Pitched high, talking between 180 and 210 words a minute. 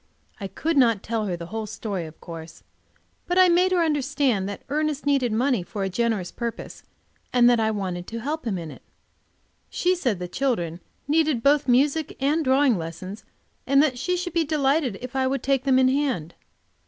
Yes: very high, 255 Hz; average, 195 wpm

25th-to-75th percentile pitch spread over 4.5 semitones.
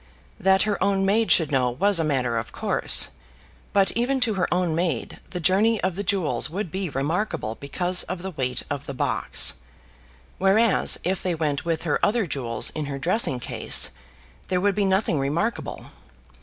Yes: wide, 5.6 semitones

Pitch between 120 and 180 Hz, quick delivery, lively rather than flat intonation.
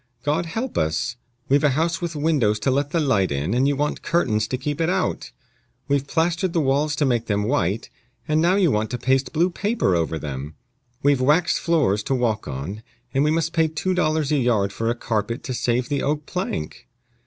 Yes: medium, 140 Hz; fast, 210 wpm; wide, 6.4 semitones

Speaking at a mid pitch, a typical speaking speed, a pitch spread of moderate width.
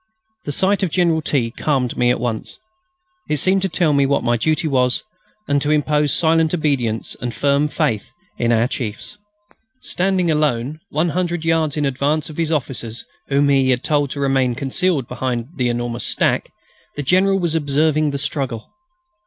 Yes: medium, 145 Hz; average, 170 wpm; average, 4.0 semitones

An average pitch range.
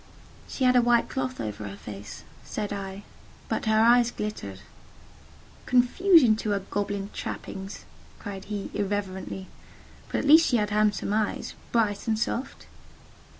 Yes: average, 3.4 semitones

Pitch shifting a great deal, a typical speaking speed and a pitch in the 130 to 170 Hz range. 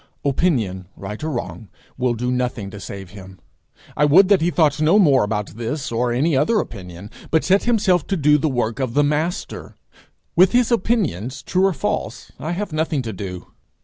Yes: wide, 7.7 semitones; average, 190 wpm; medium, 140 Hz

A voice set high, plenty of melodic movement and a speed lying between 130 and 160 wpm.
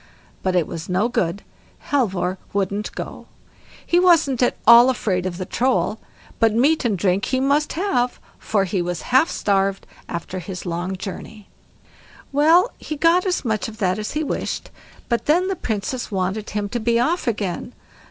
No: high, 220 Hz; wide, 6.0 semitones; average, 170 wpm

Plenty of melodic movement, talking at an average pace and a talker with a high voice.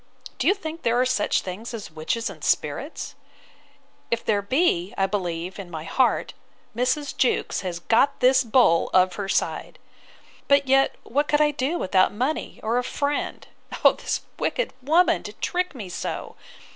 Yes: wide, 6.7 semitones; average, 165 wpm; high, 235 Hz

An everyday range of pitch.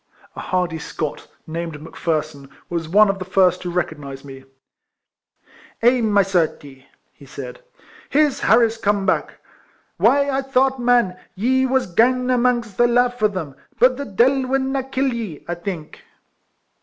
No: wide, 6.9 semitones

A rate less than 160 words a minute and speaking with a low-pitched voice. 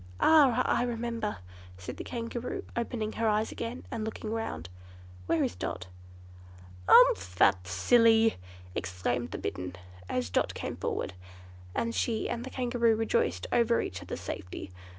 No: average, 145 wpm; high, 225 Hz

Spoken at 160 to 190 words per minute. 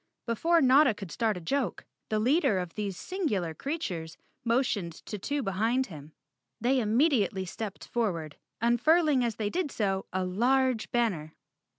No: average, 150 wpm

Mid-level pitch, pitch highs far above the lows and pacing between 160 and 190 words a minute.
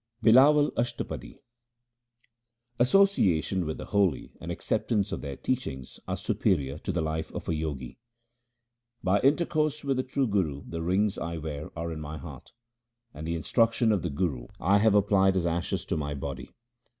No: very low, 95 Hz; wide, 6.9 semitones; average, 170 wpm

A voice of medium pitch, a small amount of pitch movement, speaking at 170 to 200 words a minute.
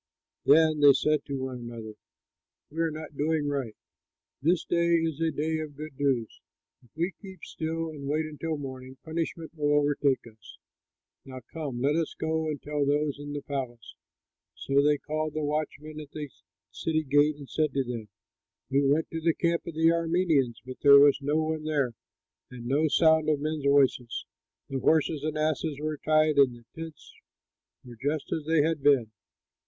Yes: medium, 150 Hz; narrow, 2.3 semitones; average, 180 wpm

